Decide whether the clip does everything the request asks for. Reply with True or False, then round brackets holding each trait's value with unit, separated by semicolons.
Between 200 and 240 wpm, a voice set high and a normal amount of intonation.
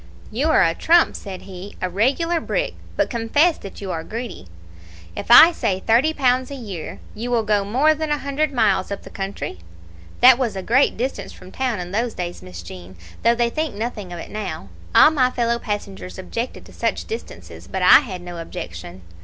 False (205 wpm; 225 Hz; 5.9 semitones)